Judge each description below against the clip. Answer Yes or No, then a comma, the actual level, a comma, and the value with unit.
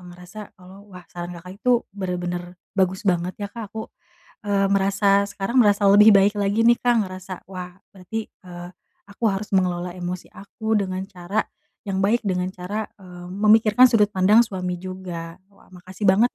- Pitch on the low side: No, high, 190 Hz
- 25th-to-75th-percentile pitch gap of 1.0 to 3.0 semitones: Yes, narrow, 2.4 semitones